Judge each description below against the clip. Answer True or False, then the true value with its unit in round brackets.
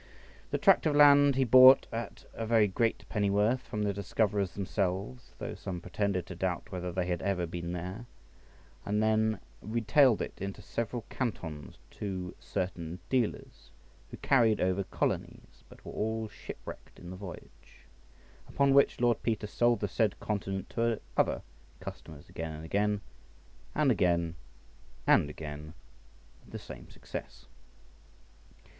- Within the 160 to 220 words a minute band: False (145 wpm)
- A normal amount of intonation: True (4.2 semitones)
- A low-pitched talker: True (100 Hz)